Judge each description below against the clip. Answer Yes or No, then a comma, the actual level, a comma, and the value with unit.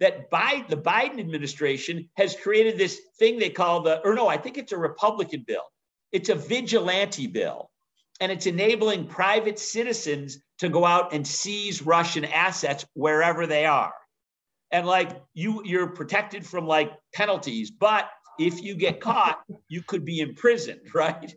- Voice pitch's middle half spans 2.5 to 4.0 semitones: No, average, 5.1 semitones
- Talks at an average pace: Yes, average, 160 wpm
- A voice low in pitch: No, medium, 185 Hz